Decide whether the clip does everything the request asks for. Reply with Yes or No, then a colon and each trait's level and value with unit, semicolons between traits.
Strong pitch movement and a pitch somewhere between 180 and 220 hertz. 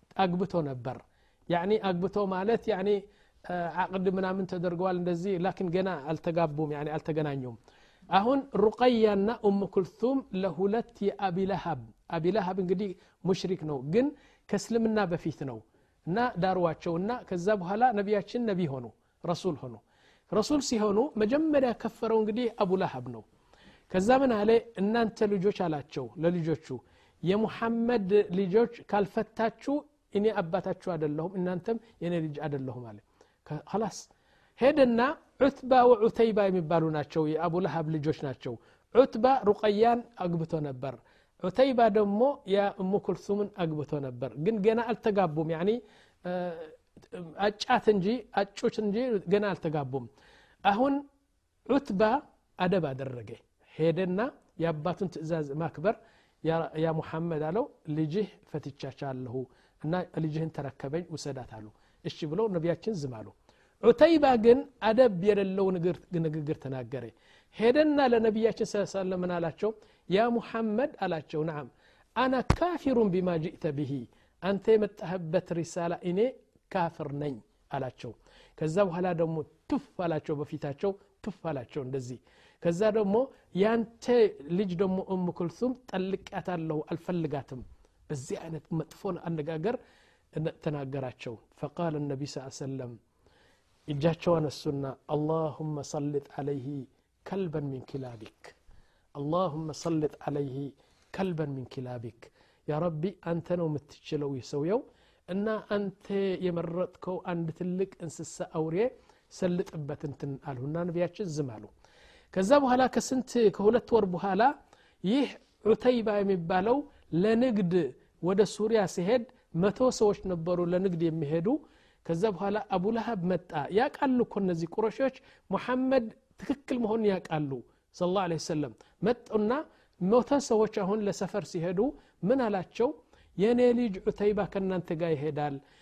Yes: wide, 5.8 semitones; medium, 185 Hz